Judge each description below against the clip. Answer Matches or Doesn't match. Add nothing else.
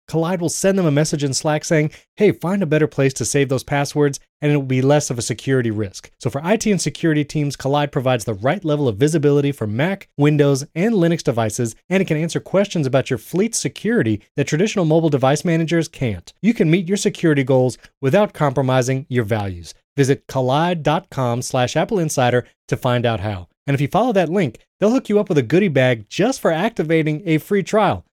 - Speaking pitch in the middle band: Matches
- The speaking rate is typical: Doesn't match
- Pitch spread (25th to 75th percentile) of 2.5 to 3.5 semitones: Doesn't match